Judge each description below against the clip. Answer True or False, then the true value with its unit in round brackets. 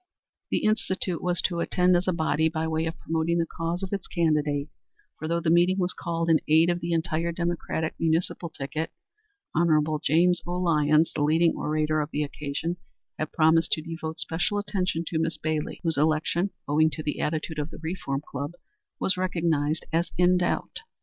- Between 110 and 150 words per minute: False (185 wpm)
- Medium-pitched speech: True (165 Hz)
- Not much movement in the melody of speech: True (1.8 semitones)